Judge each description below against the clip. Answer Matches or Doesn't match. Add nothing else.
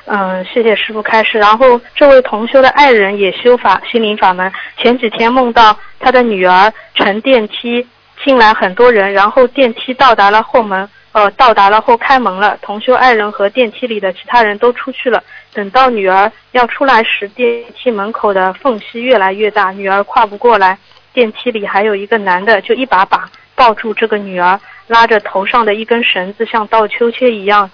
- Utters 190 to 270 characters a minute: Doesn't match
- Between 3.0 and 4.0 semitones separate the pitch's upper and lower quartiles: Matches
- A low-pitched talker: Doesn't match